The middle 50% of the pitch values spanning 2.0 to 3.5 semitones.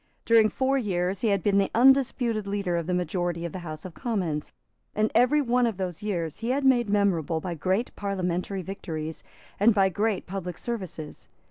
No: average, 4.4 semitones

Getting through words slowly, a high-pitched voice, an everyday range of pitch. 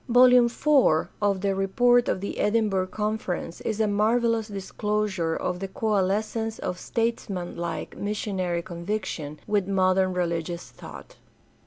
Yes: slow, 125 wpm; high, 200 Hz; average, 3.1 semitones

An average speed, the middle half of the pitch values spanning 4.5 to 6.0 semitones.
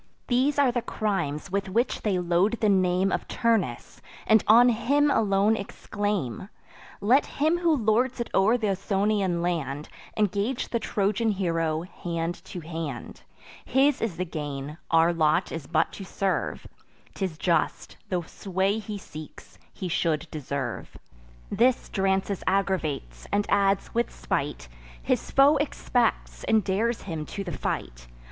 Yes: average, 145 wpm; average, 5.1 semitones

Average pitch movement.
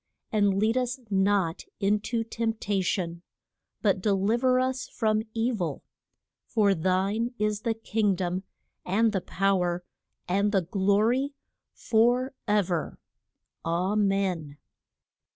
Yes: average, 3.0 semitones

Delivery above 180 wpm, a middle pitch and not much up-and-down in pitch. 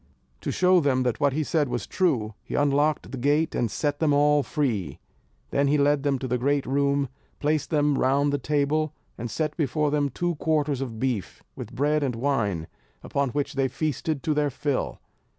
Yes: average, 195 wpm; medium, 145 Hz; narrow, 2.2 semitones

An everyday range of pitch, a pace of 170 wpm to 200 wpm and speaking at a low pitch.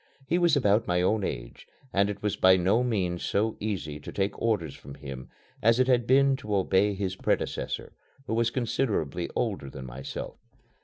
Yes: average, 4.6 semitones; average, 185 wpm; low, 100 Hz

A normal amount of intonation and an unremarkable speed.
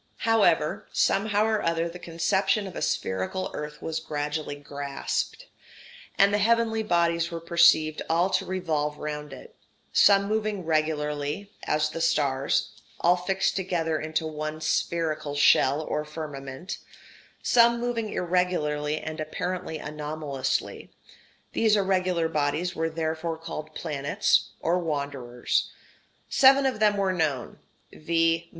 No: average, 3.7 semitones; slow, 130 wpm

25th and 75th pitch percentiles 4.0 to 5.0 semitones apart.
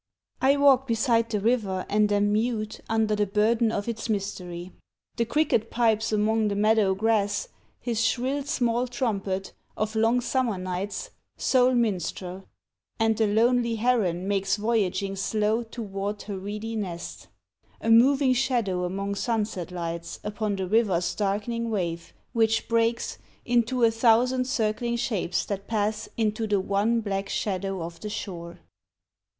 No: average, 2.8 semitones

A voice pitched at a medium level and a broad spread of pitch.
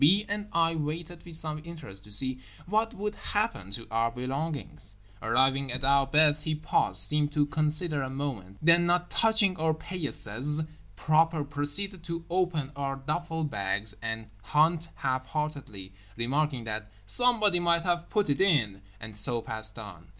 Yes: medium, 150 Hz; wide, 6.3 semitones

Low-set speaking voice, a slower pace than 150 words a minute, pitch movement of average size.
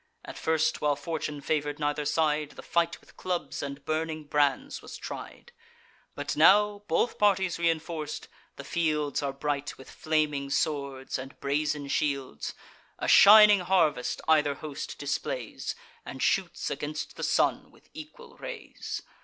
No: medium, 155 Hz; average, 140 wpm; average, 3.0 semitones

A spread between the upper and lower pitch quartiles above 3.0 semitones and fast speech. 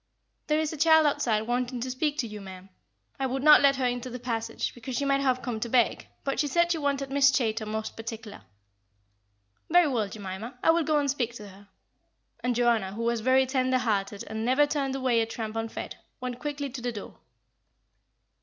Yes: average, 3.7 semitones; fast, 210 wpm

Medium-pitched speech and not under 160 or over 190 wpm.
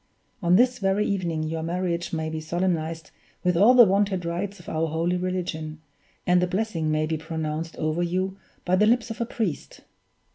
Yes: medium, 175 Hz; average, 185 wpm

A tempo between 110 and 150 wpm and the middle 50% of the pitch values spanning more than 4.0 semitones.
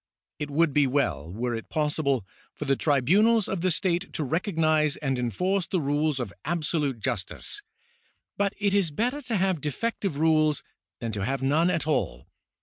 No: average, 175 wpm; average, 5.1 semitones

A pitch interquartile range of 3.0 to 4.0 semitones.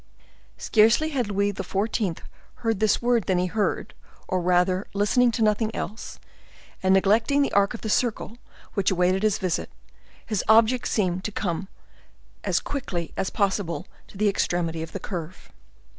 Yes: average, 3.3 semitones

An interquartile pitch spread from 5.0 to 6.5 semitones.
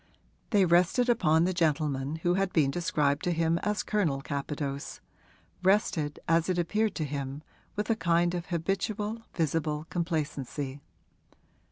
No: average, 4.0 semitones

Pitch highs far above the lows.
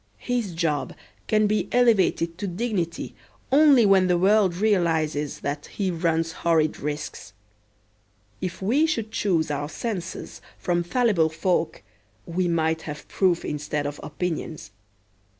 No: average, 4.4 semitones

